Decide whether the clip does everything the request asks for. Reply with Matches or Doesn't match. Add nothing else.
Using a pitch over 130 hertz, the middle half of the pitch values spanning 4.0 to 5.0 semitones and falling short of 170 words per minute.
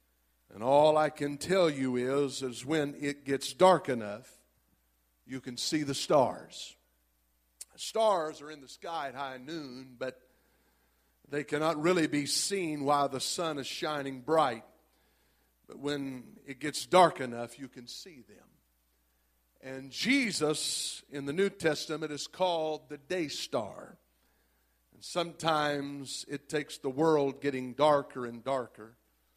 Matches